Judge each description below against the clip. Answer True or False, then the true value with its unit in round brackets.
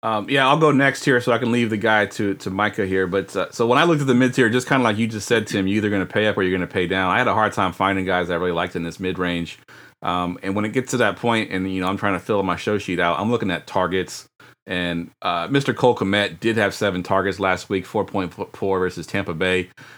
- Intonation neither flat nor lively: True (4.1 semitones)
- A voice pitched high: False (100 Hz)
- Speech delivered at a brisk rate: True (305 wpm)